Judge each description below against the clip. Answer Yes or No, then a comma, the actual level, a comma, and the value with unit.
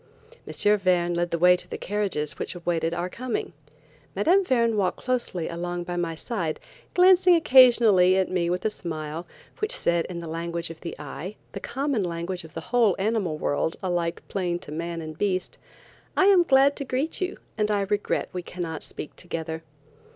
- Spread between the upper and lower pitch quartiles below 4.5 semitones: No, average, 5.2 semitones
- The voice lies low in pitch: No, medium, 180 Hz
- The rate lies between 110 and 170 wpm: No, average, 180 wpm